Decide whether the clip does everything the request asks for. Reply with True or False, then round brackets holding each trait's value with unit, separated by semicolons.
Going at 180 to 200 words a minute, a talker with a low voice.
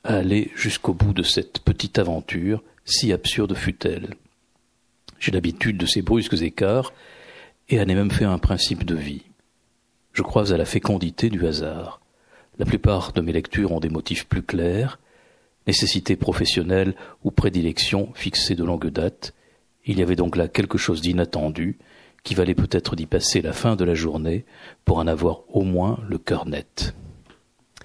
False (170 wpm; 95 Hz)